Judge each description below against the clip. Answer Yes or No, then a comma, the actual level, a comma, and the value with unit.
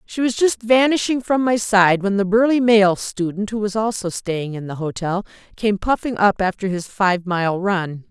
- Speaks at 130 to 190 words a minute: No, average, 200 wpm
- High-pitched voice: Yes, high, 205 Hz